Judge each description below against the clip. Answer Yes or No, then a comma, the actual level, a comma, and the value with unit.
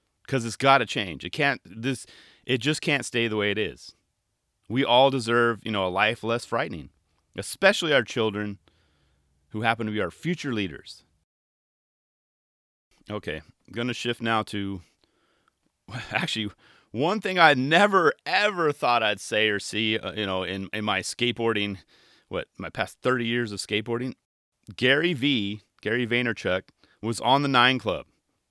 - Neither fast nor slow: Yes, average, 155 wpm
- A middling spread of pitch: Yes, average, 3.7 semitones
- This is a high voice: No, low, 110 Hz